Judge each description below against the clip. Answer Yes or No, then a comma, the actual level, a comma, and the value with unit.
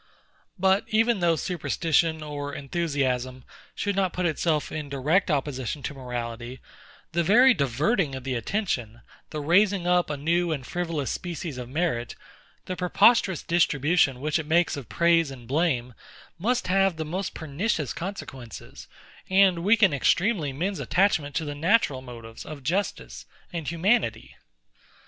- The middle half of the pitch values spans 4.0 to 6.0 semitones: Yes, average, 5.0 semitones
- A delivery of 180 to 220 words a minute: No, average, 145 wpm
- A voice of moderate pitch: Yes, medium, 160 Hz